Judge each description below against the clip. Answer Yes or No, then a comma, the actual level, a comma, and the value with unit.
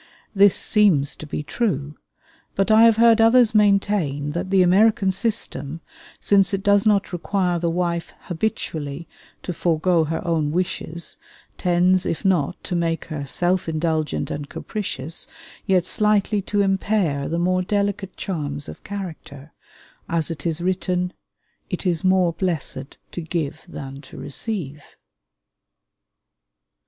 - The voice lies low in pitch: No, medium, 180 Hz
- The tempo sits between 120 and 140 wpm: Yes, slow, 135 wpm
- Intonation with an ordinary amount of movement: Yes, average, 4.0 semitones